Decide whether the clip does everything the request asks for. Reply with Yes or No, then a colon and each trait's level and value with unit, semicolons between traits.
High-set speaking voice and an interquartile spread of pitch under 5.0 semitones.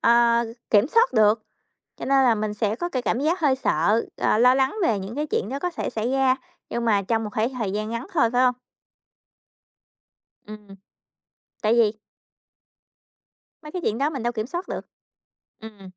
Yes: high, 235 Hz; average, 3.8 semitones